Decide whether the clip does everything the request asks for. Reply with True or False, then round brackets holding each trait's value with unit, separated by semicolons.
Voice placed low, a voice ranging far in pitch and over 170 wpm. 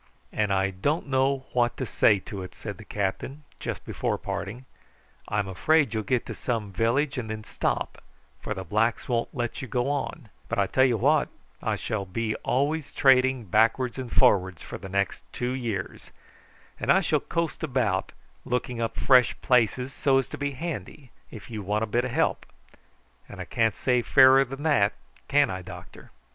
False (120 Hz; 4.1 semitones; 185 wpm)